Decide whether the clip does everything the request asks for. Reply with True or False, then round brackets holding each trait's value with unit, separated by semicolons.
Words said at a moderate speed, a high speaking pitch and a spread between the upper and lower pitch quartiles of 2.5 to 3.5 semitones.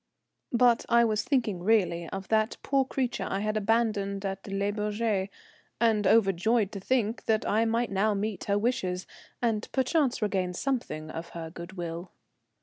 True (160 wpm; 210 Hz; 3.1 semitones)